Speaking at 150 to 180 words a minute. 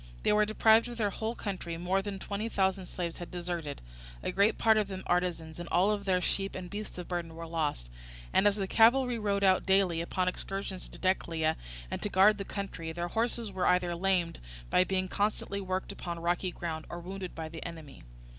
No: fast, 205 wpm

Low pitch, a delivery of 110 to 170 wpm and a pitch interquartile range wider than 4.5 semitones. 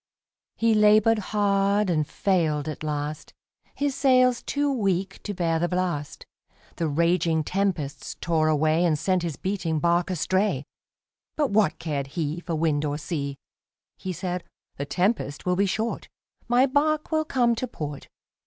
No: medium, 180 Hz; average, 155 wpm; average, 5.1 semitones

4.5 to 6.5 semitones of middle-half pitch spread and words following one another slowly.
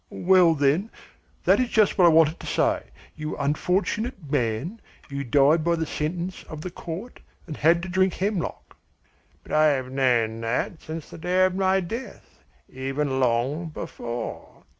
No: average, 4.9 semitones; average, 160 wpm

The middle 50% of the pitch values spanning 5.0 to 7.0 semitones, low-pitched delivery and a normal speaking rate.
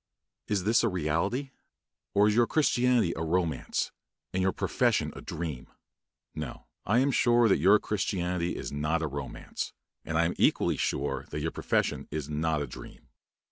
Yes: wide, 5.5 semitones; very low, 90 Hz; average, 170 wpm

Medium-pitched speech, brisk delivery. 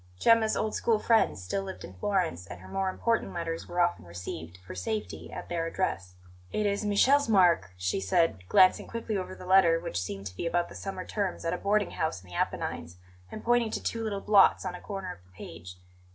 Yes: medium, 175 Hz; fast, 220 wpm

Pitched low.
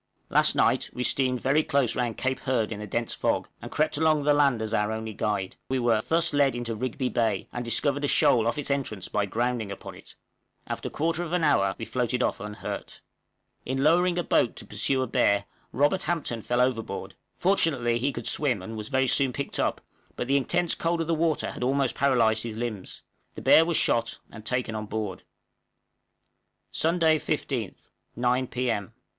Yes: low, 125 Hz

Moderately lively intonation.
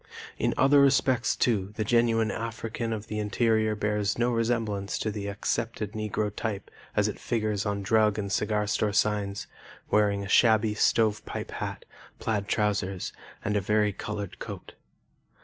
No: narrow, 1.6 semitones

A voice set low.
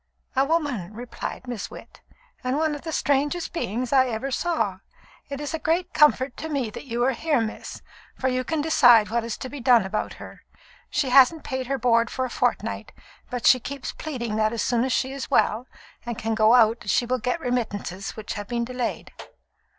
No: very high, 250 Hz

